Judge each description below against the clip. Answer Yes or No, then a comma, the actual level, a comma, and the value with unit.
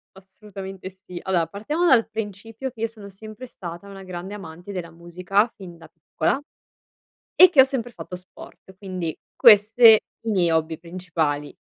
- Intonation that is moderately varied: Yes, average, 4.0 semitones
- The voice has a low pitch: No, high, 190 Hz